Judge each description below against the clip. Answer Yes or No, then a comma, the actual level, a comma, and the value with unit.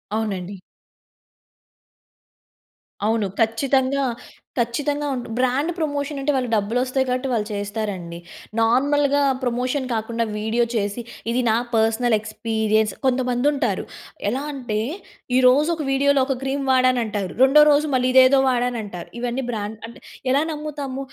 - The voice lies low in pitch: No, very high, 250 Hz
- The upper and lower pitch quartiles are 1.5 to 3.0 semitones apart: No, average, 3.7 semitones